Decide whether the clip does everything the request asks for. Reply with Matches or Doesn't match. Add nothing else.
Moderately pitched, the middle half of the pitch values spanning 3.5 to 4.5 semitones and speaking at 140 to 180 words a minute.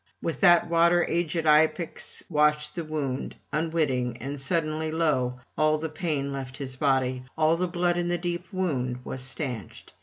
Matches